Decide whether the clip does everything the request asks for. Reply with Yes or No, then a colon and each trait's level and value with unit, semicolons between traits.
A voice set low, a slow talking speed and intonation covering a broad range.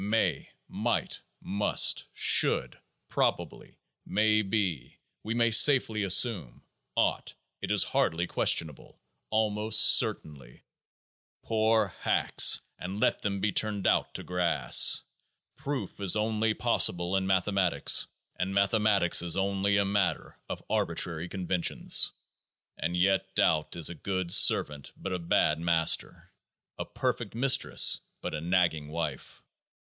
No: very low, 95 Hz; slow, 120 wpm; average, 3.9 semitones